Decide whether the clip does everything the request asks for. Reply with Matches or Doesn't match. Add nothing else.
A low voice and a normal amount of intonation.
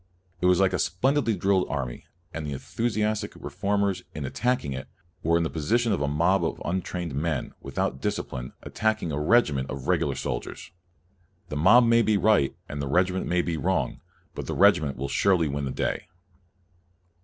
Doesn't match